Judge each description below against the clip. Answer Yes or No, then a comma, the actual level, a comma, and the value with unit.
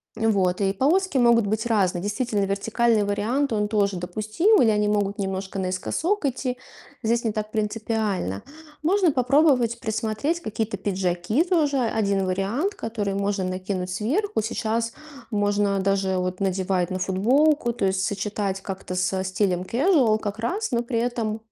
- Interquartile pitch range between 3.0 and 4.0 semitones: Yes, average, 3.6 semitones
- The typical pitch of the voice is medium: No, high, 210 Hz